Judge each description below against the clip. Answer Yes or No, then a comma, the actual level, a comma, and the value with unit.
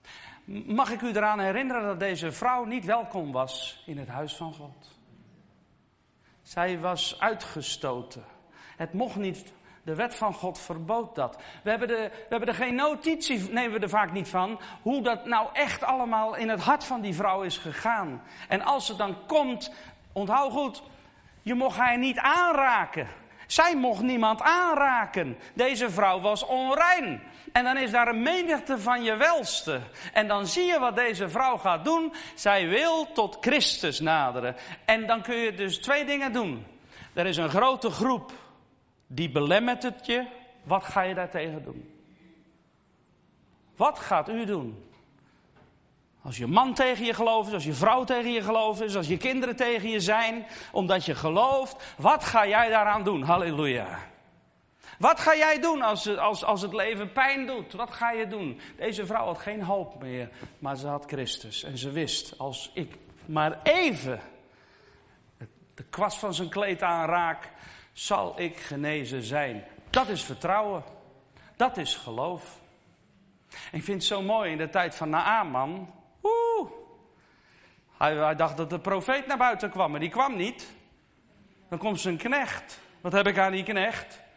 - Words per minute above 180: No, average, 165 wpm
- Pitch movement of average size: No, wide, 6.5 semitones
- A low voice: No, high, 210 Hz